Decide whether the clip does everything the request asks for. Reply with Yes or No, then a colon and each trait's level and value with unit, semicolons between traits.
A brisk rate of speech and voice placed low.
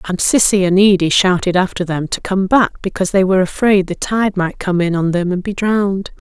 No: fast, 230 wpm; high, 190 Hz